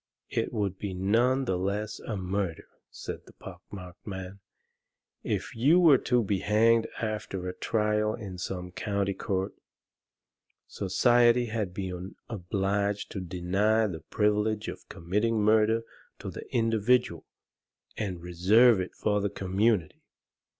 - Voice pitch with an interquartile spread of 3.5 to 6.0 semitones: No, average, 3.0 semitones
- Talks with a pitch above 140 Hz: No, low, 105 Hz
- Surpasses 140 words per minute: No, slow, 135 wpm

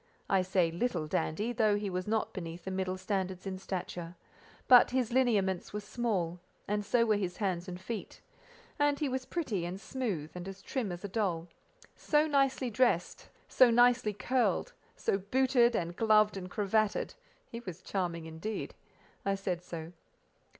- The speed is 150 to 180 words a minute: Yes, average, 165 wpm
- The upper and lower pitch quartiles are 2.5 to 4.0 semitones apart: No, average, 4.7 semitones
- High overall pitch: Yes, high, 200 Hz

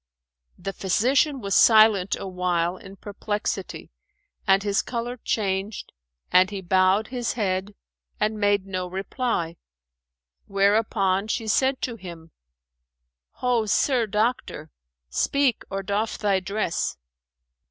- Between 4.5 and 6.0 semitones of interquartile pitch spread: No, average, 2.8 semitones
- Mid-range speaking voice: No, high, 200 Hz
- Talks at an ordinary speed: No, slow, 110 wpm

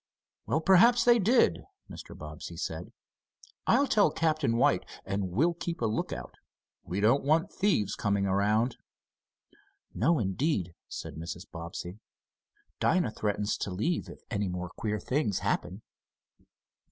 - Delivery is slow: Yes, slow, 130 wpm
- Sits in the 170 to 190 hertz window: No, low, 110 Hz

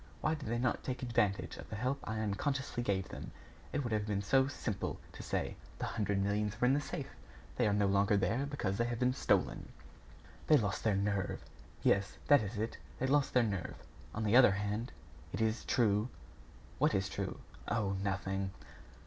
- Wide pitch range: No, average, 4.0 semitones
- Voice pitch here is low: Yes, low, 110 Hz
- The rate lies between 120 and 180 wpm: No, average, 195 wpm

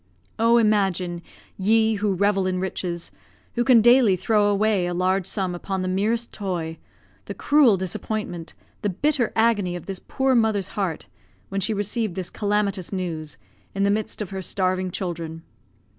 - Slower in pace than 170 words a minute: Yes, average, 160 wpm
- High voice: Yes, high, 195 Hz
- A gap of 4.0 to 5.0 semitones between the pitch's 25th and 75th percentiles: No, average, 3.0 semitones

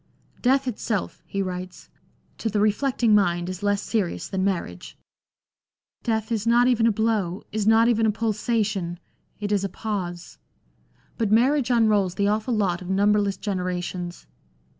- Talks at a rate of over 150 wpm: Yes, average, 160 wpm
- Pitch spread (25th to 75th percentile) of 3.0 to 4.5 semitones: Yes, average, 3.4 semitones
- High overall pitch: Yes, high, 210 Hz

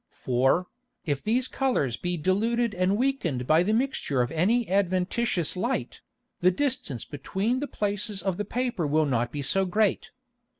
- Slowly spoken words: No, average, 160 wpm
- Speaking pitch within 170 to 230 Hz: Yes, high, 190 Hz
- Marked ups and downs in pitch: Yes, wide, 7.0 semitones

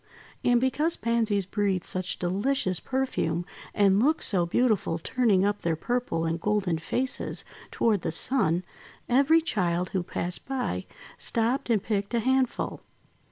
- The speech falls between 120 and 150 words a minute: Yes, average, 140 wpm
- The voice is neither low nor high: No, high, 205 Hz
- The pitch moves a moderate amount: No, wide, 5.9 semitones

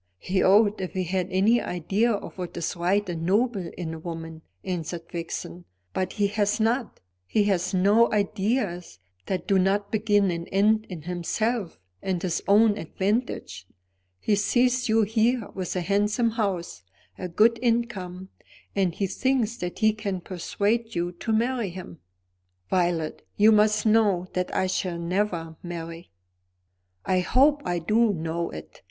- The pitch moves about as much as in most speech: Yes, average, 3.7 semitones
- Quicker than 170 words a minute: No, average, 155 wpm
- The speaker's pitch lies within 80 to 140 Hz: No, high, 195 Hz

